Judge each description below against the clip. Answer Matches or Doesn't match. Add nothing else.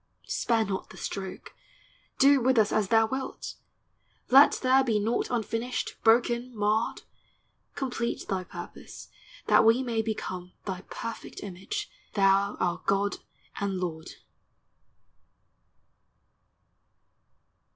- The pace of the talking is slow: Matches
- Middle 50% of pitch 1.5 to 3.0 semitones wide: Doesn't match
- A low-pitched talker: Doesn't match